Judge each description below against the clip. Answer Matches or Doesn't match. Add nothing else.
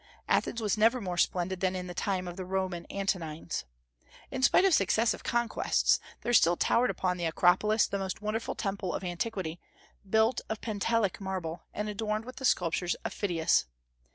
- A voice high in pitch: Matches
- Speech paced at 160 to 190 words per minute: Matches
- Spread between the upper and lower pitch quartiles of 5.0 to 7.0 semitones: Doesn't match